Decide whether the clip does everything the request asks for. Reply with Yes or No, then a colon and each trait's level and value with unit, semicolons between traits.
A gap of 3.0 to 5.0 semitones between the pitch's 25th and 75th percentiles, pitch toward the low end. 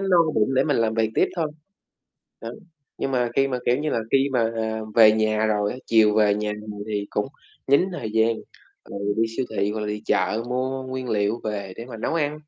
Yes: average, 3.6 semitones; low, 115 Hz